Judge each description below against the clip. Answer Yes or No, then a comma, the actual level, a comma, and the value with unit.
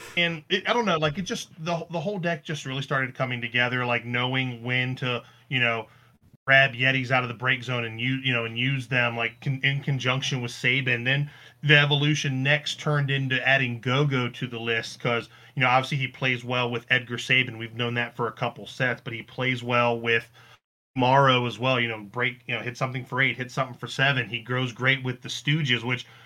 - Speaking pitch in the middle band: No, low, 125 Hz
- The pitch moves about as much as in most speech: No, narrow, 2.1 semitones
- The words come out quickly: Yes, fast, 225 wpm